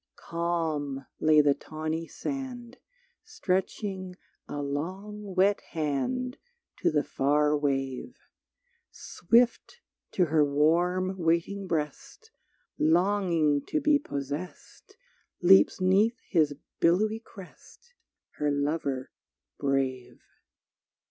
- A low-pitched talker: No, medium, 170 Hz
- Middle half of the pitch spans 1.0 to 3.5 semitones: No, wide, 5.4 semitones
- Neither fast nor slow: No, slow, 90 wpm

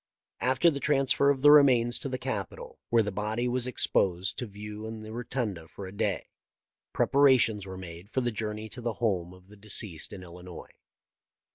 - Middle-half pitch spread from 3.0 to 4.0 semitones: No, average, 4.6 semitones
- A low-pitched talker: Yes, low, 110 Hz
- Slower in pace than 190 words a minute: No, average, 195 wpm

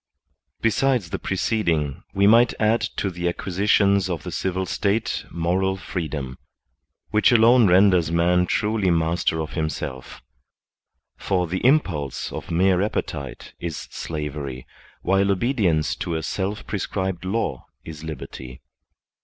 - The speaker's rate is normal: No, slow, 125 wpm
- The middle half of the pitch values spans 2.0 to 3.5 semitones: No, average, 4.1 semitones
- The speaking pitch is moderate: No, very low, 90 Hz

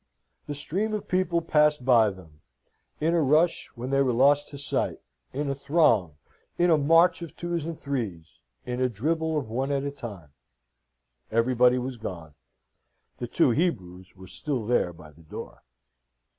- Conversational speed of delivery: Yes, average, 170 wpm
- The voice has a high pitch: No, low, 135 Hz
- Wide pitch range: Yes, wide, 6.1 semitones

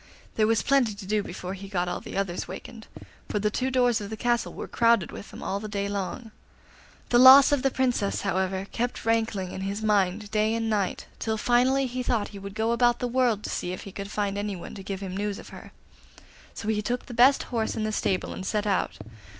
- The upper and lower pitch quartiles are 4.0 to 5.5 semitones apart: No, average, 3.4 semitones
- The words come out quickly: Yes, fast, 235 wpm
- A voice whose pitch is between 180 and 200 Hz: No, high, 215 Hz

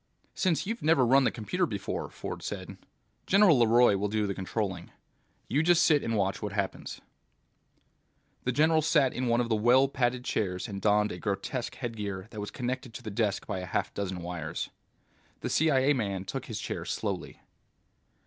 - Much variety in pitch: No, average, 5.0 semitones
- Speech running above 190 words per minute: No, average, 180 wpm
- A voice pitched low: Yes, low, 115 Hz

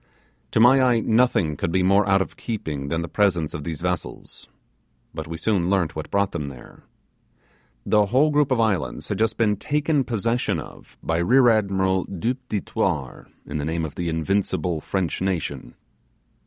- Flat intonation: No, wide, 5.6 semitones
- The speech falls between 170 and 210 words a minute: Yes, average, 180 wpm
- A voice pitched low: Yes, very low, 95 Hz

